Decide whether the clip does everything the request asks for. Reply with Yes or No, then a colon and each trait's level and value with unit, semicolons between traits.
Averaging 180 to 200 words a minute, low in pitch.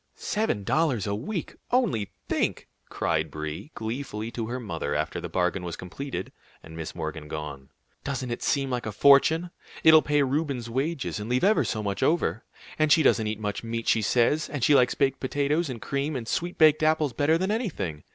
Yes: average, 195 wpm; low, 130 Hz